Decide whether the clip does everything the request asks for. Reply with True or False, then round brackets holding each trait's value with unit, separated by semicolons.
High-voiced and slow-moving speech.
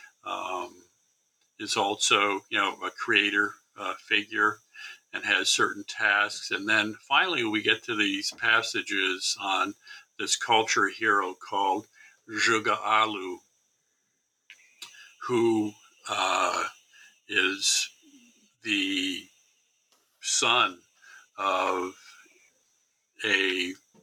True (300 Hz; 85 wpm)